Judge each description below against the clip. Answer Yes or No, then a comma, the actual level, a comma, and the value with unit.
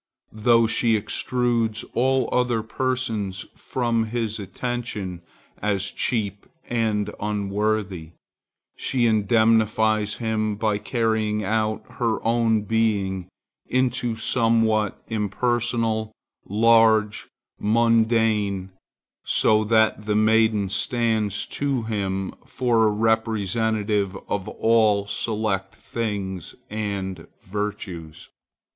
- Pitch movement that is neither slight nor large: No, narrow, 1.9 semitones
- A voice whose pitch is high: No, low, 110 Hz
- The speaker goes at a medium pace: No, slow, 90 wpm